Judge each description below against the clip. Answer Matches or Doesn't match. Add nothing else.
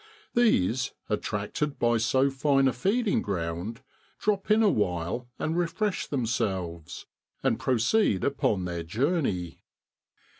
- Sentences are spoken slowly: Matches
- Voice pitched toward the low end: Matches